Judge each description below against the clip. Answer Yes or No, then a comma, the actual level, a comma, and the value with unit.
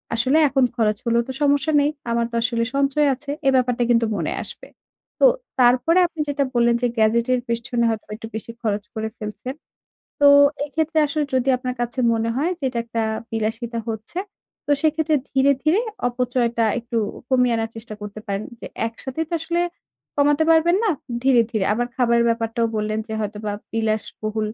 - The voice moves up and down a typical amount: Yes, average, 3.8 semitones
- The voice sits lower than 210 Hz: No, high, 240 Hz